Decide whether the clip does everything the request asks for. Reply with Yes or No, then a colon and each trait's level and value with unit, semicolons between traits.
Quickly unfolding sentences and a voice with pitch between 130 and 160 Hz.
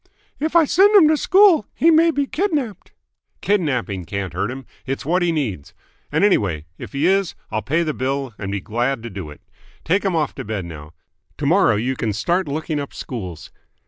Yes: fast, 210 wpm; medium, 140 Hz